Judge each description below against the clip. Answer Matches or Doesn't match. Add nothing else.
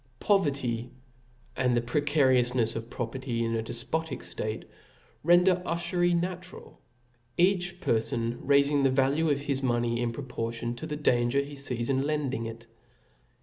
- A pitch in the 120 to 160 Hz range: Matches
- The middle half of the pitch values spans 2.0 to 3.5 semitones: Doesn't match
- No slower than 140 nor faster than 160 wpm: Matches